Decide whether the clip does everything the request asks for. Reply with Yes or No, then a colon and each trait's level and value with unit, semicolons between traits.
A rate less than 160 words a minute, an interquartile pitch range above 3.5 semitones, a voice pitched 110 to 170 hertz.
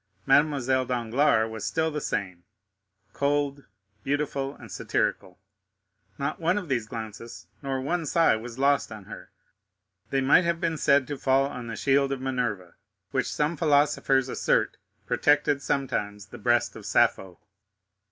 Yes: average, 140 wpm; average, 4.3 semitones; low, 135 Hz